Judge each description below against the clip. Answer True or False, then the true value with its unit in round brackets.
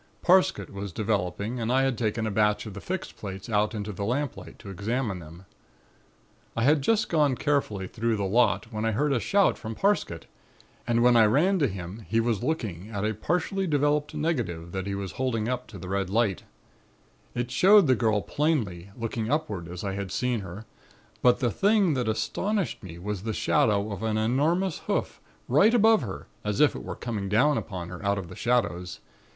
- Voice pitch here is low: True (110 Hz)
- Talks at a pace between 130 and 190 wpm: False (200 wpm)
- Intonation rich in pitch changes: True (5.8 semitones)